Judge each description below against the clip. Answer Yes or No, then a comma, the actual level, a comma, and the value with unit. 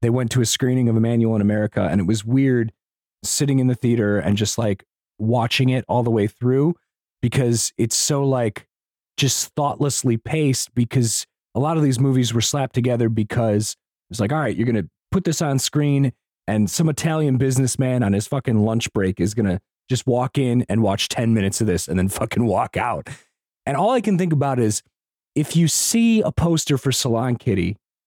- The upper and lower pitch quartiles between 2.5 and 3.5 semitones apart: No, average, 3.9 semitones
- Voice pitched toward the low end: Yes, low, 120 Hz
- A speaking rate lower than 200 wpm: No, fast, 205 wpm